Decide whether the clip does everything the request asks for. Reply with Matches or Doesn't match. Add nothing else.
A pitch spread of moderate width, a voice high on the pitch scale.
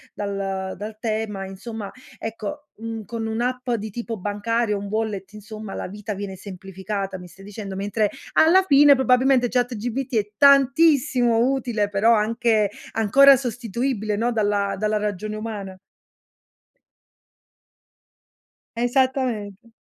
Matches